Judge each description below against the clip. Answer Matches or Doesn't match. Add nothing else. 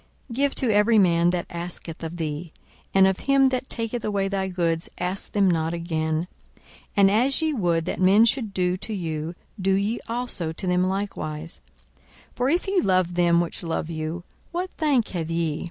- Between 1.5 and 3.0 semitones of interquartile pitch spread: Doesn't match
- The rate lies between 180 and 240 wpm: Matches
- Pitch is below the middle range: Doesn't match